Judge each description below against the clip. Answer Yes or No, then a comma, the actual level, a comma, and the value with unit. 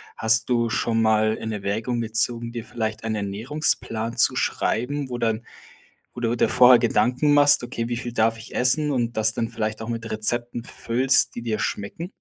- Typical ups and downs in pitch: No, narrow, 1.8 semitones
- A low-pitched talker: Yes, low, 115 Hz